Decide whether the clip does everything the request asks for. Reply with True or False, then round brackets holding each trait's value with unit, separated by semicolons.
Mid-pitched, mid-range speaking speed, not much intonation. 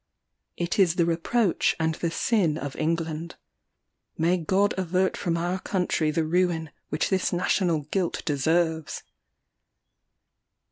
False (170 Hz; 125 wpm; 2.2 semitones)